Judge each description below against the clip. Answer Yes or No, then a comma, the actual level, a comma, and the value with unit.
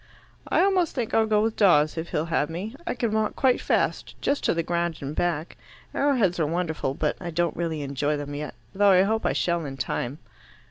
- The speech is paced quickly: Yes, fast, 220 wpm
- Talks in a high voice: No, medium, 170 Hz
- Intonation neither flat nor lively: No, wide, 6.1 semitones